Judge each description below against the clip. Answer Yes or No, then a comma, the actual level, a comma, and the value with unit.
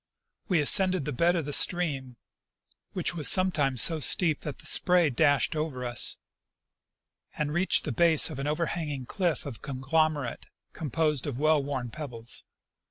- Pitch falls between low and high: Yes, medium, 150 Hz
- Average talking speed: Yes, average, 160 wpm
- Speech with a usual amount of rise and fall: Yes, average, 3.7 semitones